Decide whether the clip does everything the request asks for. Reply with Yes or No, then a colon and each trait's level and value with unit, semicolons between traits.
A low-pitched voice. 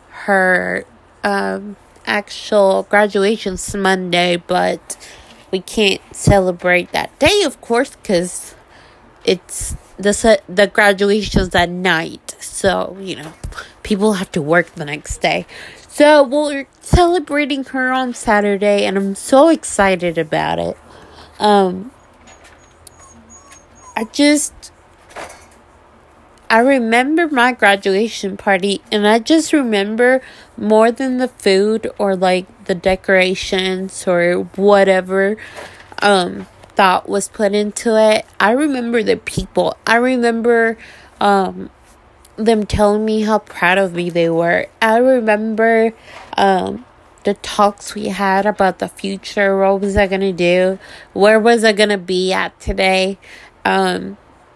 No: high, 200 Hz